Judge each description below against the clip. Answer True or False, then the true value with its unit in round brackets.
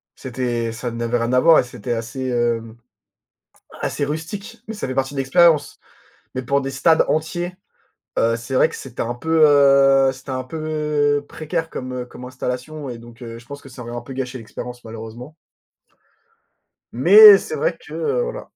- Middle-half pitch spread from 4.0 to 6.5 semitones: True (4.3 semitones)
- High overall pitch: False (135 Hz)